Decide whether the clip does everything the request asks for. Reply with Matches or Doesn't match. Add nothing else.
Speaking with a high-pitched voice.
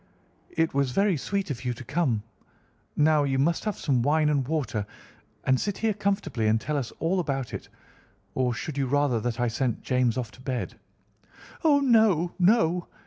Doesn't match